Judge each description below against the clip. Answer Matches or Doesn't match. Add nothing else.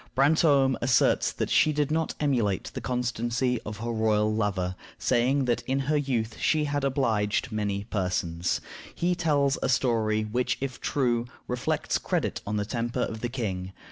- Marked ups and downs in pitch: Doesn't match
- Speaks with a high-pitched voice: Doesn't match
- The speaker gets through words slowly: Doesn't match